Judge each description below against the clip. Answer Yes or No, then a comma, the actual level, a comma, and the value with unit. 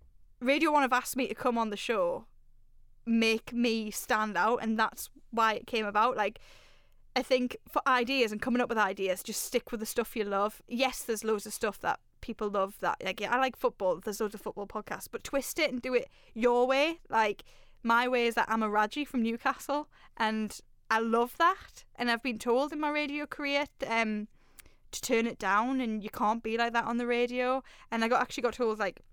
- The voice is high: Yes, high, 235 Hz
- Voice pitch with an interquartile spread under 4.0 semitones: Yes, average, 2.8 semitones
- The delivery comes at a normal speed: No, fast, 220 wpm